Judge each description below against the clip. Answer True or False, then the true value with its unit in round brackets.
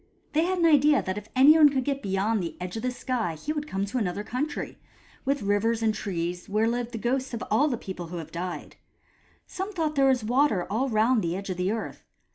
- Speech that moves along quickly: True (240 wpm)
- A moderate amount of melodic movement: False (5.9 semitones)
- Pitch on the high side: True (225 Hz)